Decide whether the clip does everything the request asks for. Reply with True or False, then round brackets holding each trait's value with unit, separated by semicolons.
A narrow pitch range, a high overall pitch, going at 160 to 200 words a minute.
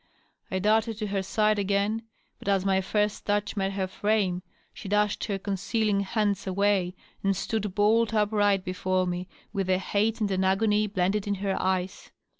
True (1.8 semitones; 200 Hz; 175 wpm)